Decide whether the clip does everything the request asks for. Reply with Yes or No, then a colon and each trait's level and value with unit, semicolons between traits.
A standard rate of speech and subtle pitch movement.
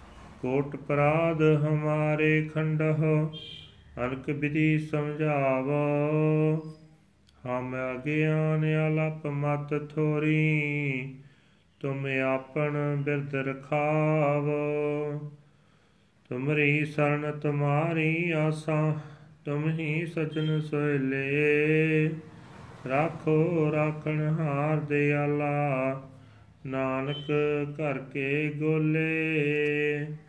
No: slow, 65 wpm; narrow, 1.2 semitones